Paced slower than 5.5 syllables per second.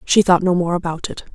No: 6.0 syllables/s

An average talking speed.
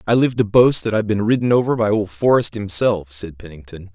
No: fast, 230 wpm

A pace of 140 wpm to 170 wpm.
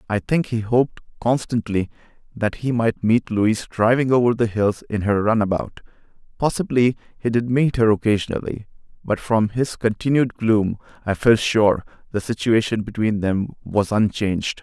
Yes: average, 150 wpm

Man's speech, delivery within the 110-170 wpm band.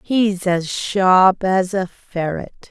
No: female; slow, 135 wpm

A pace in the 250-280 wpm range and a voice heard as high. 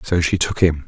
No: fast, 275 wpm; very low, 85 Hz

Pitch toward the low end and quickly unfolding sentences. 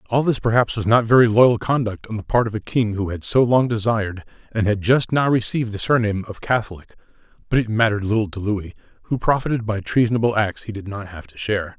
Yes: low, 110 Hz; fast, 230 wpm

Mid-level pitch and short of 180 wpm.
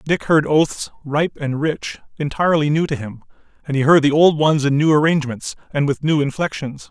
No: medium, 150 Hz; average, 200 wpm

